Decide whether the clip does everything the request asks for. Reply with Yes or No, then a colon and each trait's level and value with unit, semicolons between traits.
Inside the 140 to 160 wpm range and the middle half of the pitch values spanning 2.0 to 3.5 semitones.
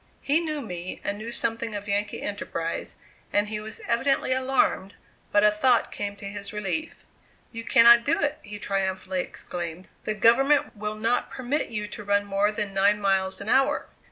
No: average, 180 wpm; average, 3.0 semitones